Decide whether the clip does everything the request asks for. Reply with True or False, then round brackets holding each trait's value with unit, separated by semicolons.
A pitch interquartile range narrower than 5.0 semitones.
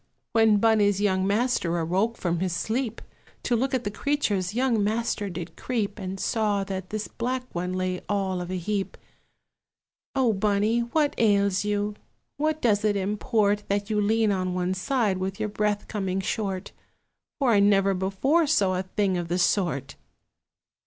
True (2.9 semitones)